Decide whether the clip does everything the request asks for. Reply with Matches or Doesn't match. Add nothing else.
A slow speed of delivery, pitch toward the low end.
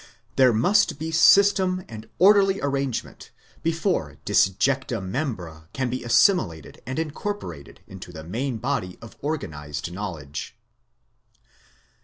Matches